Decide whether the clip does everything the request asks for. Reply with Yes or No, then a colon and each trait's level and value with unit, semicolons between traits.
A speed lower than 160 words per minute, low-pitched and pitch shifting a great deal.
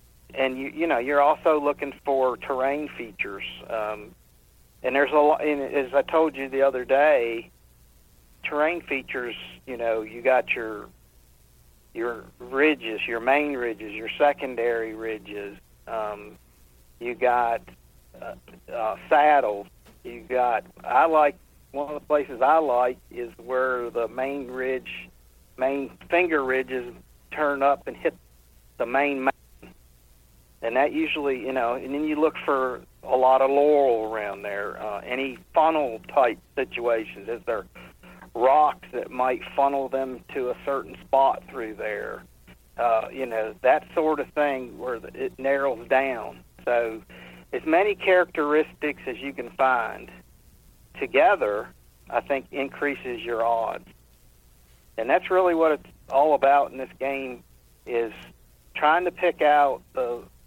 Yes: average, 140 wpm; low, 130 Hz; wide, 6.1 semitones